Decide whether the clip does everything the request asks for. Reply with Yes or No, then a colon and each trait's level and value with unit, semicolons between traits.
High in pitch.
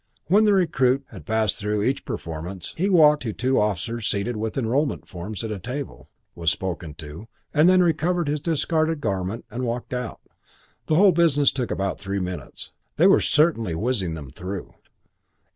No: low, 120 Hz